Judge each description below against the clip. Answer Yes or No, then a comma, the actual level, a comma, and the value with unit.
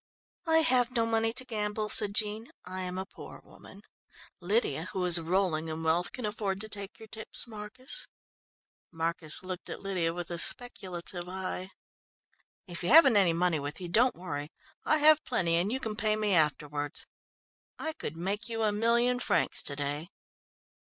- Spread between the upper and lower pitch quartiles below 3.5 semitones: No, average, 4.8 semitones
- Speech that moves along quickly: No, average, 175 wpm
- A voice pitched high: Yes, high, 195 Hz